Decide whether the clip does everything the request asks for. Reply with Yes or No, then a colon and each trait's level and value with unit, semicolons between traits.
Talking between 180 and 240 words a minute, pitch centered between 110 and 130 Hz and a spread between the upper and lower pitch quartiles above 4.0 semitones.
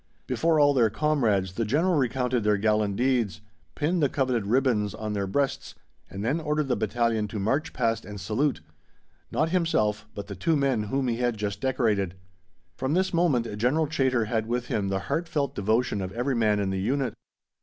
Yes: average, 185 wpm; low, 120 Hz; average, 5.0 semitones